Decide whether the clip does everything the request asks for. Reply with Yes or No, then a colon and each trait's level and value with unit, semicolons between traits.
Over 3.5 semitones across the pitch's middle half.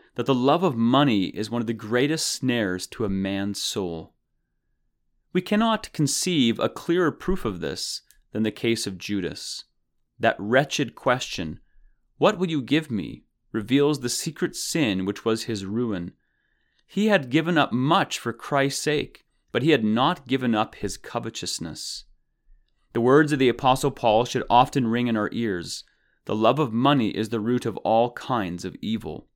Yes: average, 4.8 semitones